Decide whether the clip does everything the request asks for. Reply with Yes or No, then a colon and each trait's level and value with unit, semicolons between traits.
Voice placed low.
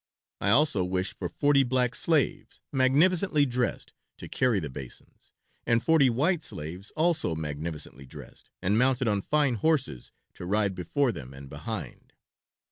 Yes: low, 120 Hz